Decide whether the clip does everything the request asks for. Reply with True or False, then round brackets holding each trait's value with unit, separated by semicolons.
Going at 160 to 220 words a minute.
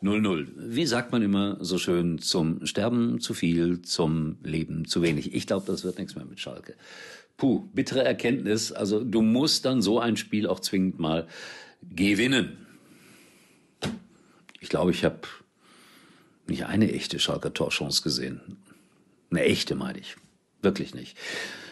False (145 wpm)